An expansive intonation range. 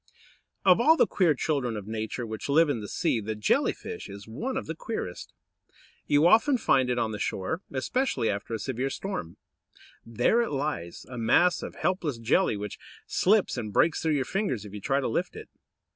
Yes: wide, 8.3 semitones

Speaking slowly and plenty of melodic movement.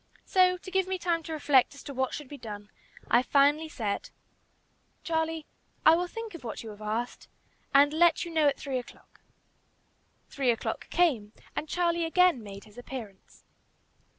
No: average, 175 wpm; wide, 5.9 semitones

